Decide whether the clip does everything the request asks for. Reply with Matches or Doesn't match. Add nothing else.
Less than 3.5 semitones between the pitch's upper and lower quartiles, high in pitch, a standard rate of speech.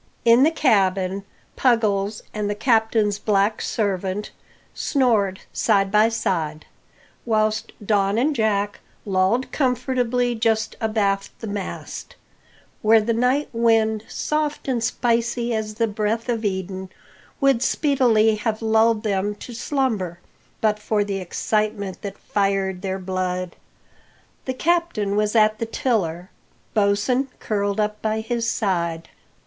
Doesn't match